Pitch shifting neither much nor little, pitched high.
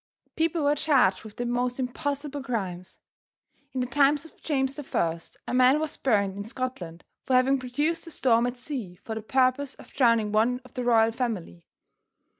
Yes: average, 3.8 semitones; very high, 250 Hz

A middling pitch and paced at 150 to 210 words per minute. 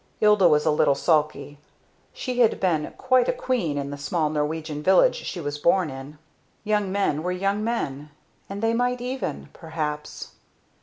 Yes: medium, 170 Hz; average, 165 wpm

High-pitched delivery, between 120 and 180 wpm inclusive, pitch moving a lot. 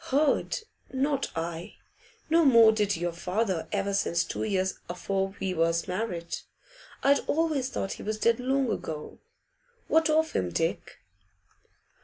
Yes: high, 205 Hz; average, 140 wpm; wide, 7.5 semitones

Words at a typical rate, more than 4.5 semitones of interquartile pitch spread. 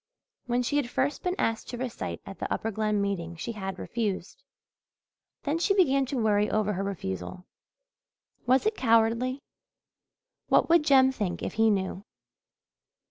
Yes: average, 155 wpm; average, 4.9 semitones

